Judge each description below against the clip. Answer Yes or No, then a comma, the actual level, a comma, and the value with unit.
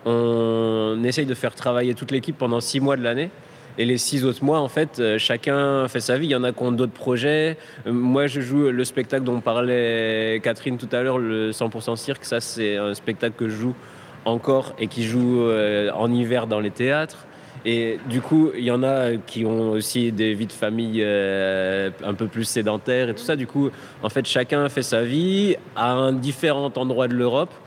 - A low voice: Yes, low, 125 Hz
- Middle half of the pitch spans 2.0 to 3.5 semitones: Yes, average, 2.9 semitones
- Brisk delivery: No, average, 210 wpm